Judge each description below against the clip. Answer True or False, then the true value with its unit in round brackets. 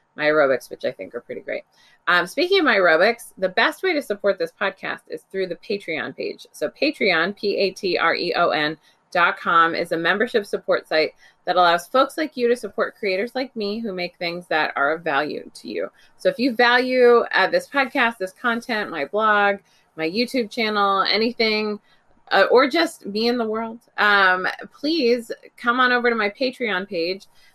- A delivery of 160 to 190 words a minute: False (200 wpm)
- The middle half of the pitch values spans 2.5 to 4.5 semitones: False (4.9 semitones)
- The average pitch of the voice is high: True (215 Hz)